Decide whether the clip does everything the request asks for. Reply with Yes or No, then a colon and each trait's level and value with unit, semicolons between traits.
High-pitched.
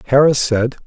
No: low, 130 Hz